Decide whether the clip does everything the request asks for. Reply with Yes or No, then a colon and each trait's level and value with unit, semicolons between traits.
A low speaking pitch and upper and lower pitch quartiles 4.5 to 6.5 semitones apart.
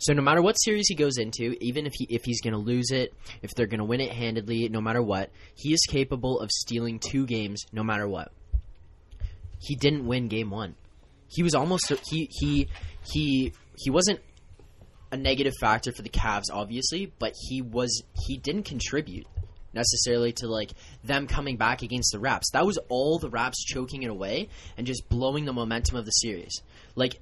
Yes: low, 115 Hz; average, 4.8 semitones